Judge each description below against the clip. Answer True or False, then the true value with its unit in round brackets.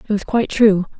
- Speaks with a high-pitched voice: True (205 Hz)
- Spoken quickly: True (240 wpm)